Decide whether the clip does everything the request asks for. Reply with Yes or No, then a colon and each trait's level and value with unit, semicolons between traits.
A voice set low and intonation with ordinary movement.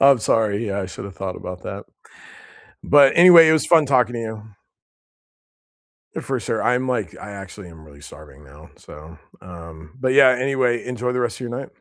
No: low, 115 Hz; wide, 6.3 semitones